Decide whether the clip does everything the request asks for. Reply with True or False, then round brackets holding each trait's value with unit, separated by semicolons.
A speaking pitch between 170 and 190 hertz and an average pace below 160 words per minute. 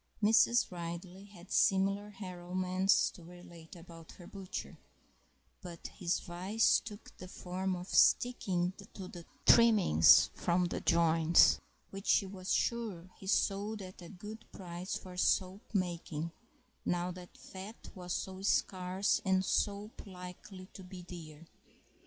True (185 Hz; 135 wpm)